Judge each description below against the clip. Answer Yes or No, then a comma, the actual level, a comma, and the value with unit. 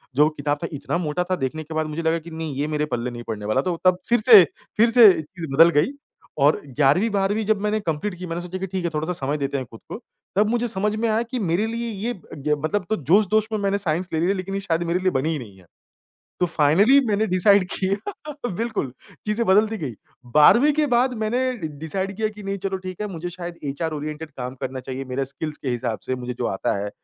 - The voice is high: No, medium, 175 Hz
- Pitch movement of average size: No, wide, 5.7 semitones